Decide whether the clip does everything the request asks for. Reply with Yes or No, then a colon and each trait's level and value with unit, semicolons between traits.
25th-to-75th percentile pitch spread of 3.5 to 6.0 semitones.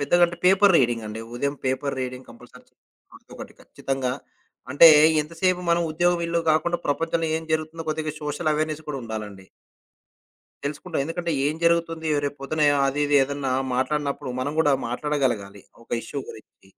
Yes: average, 4.0 semitones